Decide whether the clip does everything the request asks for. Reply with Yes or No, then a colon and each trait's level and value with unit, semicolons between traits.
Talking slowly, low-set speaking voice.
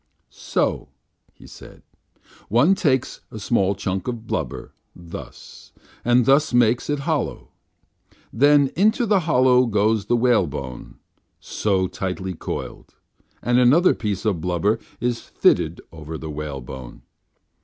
Yes: slow, 125 wpm; low, 110 Hz